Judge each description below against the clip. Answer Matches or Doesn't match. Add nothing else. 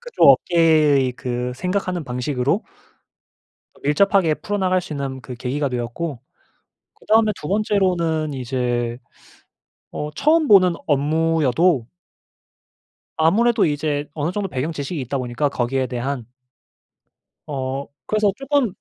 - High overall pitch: Doesn't match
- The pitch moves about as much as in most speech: Doesn't match